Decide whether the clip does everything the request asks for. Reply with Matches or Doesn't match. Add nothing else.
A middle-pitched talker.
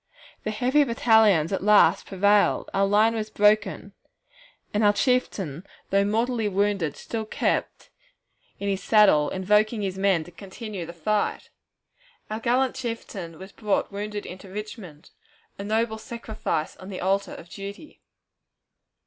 Doesn't match